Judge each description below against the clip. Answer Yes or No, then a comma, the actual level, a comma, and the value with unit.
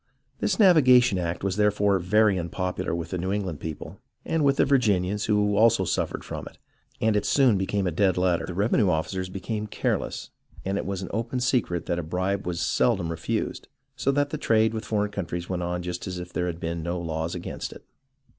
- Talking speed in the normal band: No, fast, 210 wpm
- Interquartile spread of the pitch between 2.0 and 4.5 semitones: Yes, average, 3.6 semitones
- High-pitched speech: No, very low, 95 Hz